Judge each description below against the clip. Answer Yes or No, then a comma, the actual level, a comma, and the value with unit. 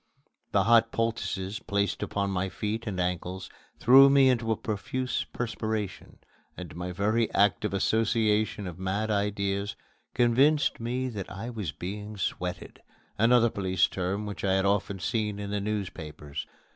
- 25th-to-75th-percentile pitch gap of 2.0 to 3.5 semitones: Yes, average, 2.9 semitones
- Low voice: Yes, low, 105 Hz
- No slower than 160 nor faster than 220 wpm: No, average, 145 wpm